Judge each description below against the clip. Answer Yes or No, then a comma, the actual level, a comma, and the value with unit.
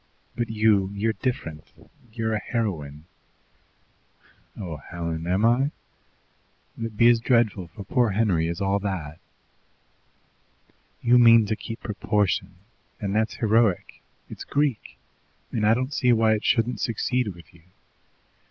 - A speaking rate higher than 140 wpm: No, slow, 135 wpm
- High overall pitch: No, low, 110 Hz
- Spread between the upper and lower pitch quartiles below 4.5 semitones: Yes, average, 3.7 semitones